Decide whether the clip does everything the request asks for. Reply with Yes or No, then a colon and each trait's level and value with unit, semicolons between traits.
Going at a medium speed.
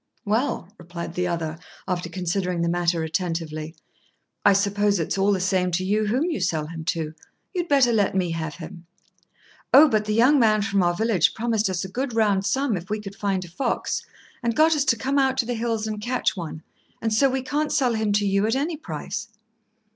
No: fast, 215 wpm